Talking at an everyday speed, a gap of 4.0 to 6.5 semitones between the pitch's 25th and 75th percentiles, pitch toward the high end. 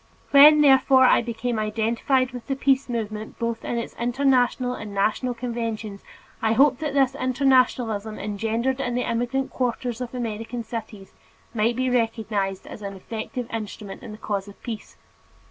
No: average, 160 wpm; average, 2.8 semitones; high, 235 Hz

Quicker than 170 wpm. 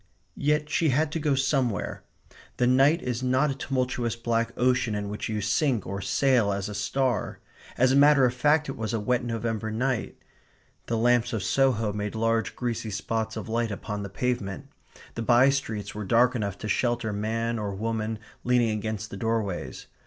Yes: average, 185 wpm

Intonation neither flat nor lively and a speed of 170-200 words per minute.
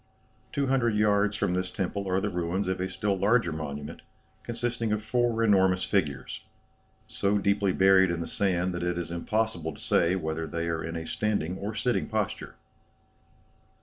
Yes: average, 3.7 semitones; average, 175 wpm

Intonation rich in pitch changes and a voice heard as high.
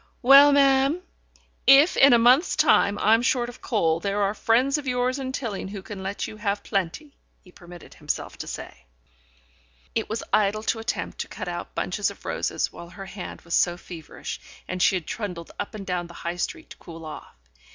Yes: wide, 5.9 semitones; high, 210 Hz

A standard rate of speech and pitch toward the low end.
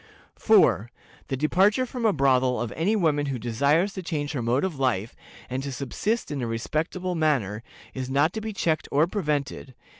No: average, 185 wpm; medium, 145 Hz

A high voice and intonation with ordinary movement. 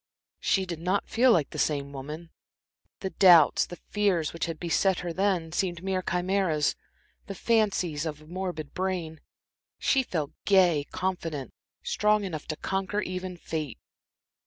No: medium, 180 Hz; average, 3.3 semitones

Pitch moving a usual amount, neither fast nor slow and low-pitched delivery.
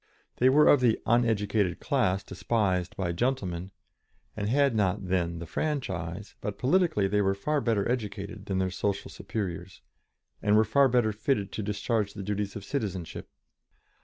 Yes: average, 3.7 semitones; average, 160 wpm; low, 105 Hz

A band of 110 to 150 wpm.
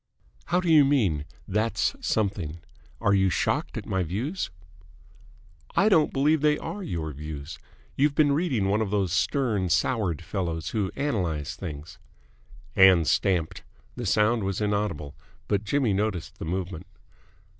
Yes: average, 145 wpm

